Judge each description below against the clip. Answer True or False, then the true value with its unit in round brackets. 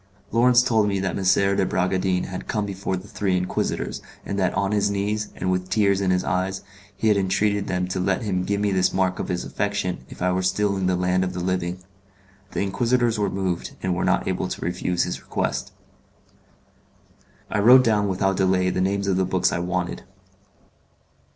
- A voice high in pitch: False (95 Hz)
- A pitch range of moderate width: False (1.7 semitones)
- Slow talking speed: False (200 wpm)